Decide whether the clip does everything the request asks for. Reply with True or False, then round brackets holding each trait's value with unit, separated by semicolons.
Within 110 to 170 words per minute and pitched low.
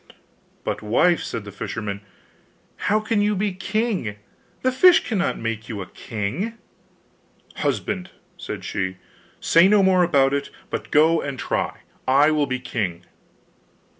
False (140 wpm; 150 Hz)